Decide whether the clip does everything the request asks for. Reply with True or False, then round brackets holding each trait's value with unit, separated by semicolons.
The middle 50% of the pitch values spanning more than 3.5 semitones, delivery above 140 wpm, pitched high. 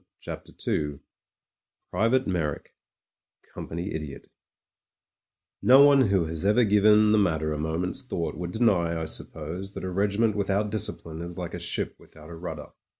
False (4.5 semitones; 150 wpm; 90 Hz)